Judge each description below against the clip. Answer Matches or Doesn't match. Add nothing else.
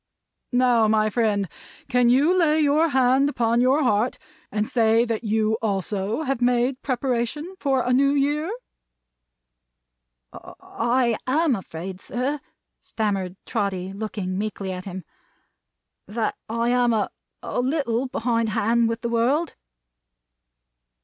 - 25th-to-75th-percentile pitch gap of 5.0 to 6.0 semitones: Doesn't match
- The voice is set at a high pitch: Matches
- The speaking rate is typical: Doesn't match